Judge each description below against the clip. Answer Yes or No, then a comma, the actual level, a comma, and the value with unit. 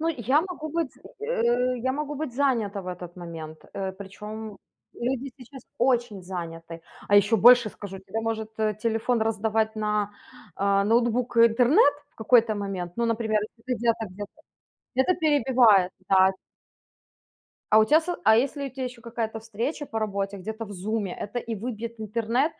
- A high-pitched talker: Yes, high, 225 Hz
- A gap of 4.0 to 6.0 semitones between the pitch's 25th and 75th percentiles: No, average, 3.6 semitones